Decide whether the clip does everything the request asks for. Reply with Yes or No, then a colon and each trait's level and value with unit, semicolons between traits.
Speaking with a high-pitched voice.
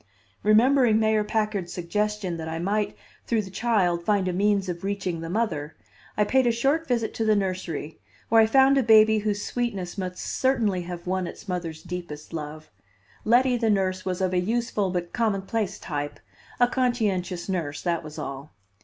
Yes: high, 195 Hz